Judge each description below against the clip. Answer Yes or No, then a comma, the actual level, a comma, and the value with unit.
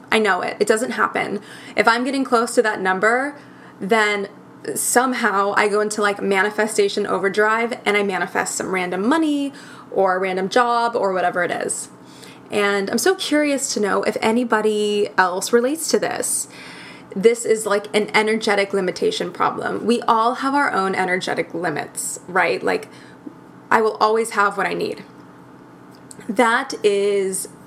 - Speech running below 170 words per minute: Yes, average, 155 wpm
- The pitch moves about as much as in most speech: Yes, average, 3.3 semitones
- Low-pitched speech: No, high, 215 Hz